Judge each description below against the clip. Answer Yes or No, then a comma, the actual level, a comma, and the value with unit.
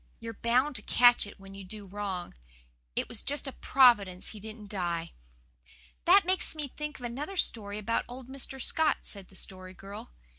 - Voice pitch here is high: Yes, high, 225 Hz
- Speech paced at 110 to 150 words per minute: No, average, 185 wpm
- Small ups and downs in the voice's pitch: No, average, 5.3 semitones